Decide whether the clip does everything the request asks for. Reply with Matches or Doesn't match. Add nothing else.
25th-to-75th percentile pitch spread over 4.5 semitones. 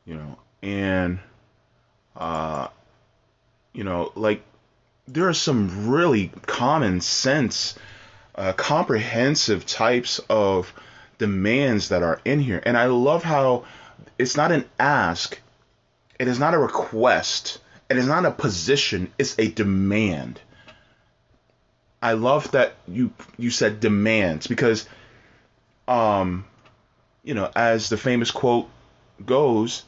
Doesn't match